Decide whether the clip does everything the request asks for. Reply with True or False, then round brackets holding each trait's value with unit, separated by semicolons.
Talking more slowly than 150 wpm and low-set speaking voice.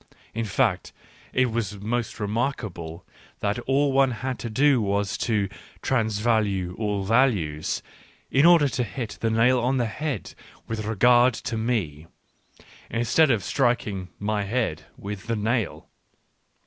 True (140 wpm; 115 Hz)